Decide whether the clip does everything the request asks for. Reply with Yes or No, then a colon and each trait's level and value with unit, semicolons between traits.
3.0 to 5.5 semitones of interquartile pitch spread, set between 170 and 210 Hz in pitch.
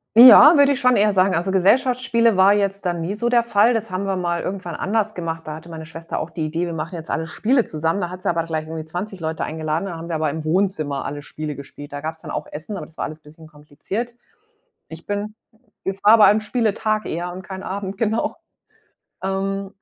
Yes: average, 4.4 semitones; medium, 185 Hz